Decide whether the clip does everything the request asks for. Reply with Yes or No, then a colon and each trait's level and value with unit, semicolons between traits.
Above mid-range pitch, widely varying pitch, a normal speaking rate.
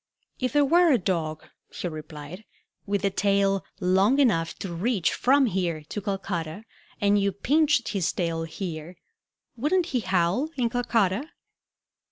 Yes: high, 195 Hz; wide, 6.2 semitones; average, 145 wpm